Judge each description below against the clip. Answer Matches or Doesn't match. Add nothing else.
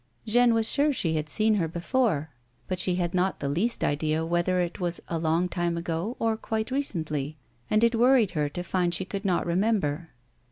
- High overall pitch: Doesn't match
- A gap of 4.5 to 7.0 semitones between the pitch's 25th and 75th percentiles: Matches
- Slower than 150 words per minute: Doesn't match